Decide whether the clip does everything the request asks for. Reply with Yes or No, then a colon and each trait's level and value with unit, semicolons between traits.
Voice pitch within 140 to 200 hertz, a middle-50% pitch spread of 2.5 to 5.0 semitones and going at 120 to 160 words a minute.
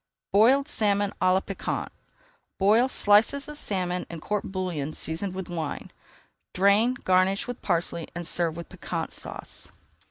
Yes: high, 190 Hz; average, 3.3 semitones; average, 145 wpm